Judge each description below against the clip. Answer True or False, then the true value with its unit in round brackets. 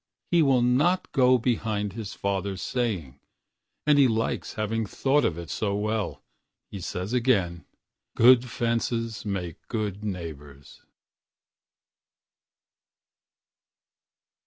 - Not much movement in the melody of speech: False (4.2 semitones)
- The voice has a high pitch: False (110 Hz)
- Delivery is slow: True (95 wpm)